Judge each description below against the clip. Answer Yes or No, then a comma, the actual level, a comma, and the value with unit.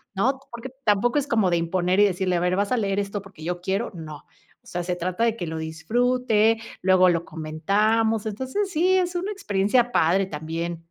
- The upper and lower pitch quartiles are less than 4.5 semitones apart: No, average, 5.0 semitones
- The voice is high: Yes, high, 195 Hz